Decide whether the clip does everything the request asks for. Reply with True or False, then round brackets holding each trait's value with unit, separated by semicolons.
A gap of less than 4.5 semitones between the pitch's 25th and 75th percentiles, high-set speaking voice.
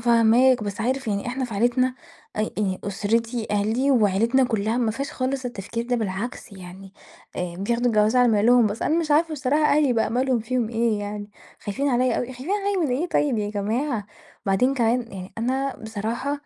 True (3.5 semitones; 235 Hz)